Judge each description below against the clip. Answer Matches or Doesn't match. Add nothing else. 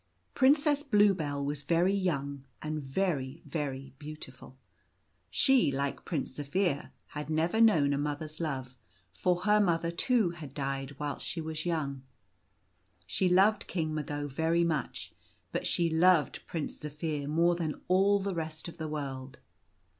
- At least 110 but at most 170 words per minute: Matches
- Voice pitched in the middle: Matches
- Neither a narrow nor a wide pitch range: Matches